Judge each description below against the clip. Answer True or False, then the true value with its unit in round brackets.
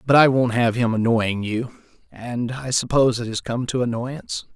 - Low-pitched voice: True (120 Hz)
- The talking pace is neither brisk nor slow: True (170 wpm)